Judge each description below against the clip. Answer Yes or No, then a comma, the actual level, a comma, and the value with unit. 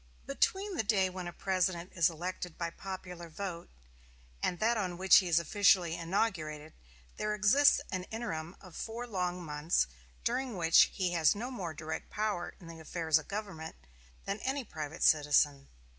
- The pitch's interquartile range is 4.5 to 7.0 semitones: No, average, 4.0 semitones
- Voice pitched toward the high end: No, medium, 180 Hz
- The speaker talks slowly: No, average, 165 wpm